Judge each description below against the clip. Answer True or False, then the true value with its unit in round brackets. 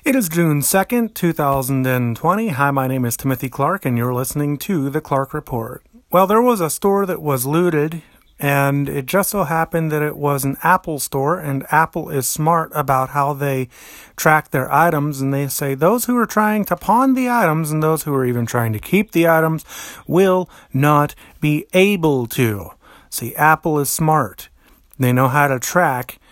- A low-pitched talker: False (150 Hz)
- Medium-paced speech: True (185 wpm)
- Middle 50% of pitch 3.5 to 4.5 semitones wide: True (4.0 semitones)